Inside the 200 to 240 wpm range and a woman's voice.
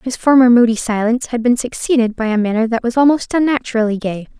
Yes: fast, 205 wpm; female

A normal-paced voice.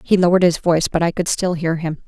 No: fast, 290 wpm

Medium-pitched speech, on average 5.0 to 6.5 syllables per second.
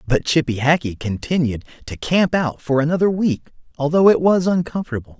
Yes: medium, 150 Hz; 5.4 syllables/s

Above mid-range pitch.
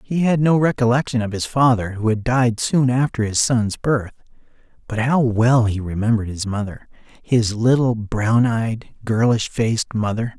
No: low, 115 Hz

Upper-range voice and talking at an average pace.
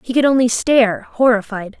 Yes: high, 235 Hz; average, 165 wpm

